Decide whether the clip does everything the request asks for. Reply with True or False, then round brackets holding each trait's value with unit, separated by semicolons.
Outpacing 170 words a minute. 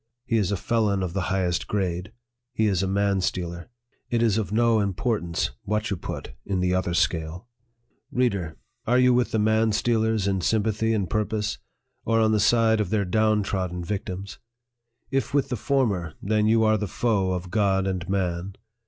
True (190 wpm)